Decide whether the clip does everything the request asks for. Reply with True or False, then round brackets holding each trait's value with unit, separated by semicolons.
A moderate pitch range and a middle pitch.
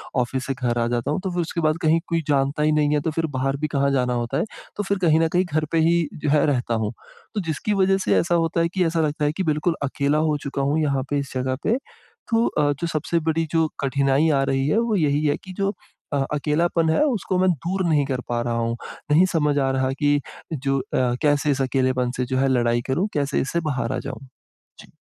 True (3.7 semitones; 150 Hz)